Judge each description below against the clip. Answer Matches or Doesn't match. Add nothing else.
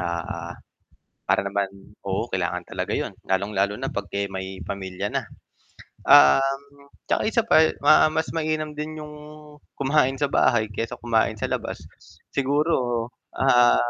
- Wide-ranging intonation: Matches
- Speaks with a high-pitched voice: Doesn't match